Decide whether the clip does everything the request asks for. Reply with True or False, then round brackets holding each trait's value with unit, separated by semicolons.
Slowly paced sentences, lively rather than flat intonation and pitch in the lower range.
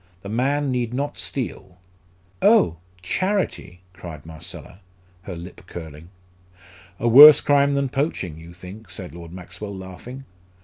True (130 wpm; 7.6 semitones; 95 Hz)